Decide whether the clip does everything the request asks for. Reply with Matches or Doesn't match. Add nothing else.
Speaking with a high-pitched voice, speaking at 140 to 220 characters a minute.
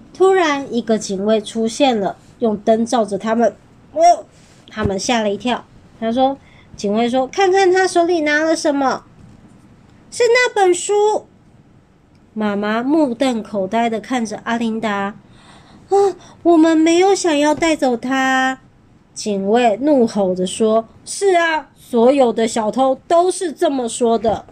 Matches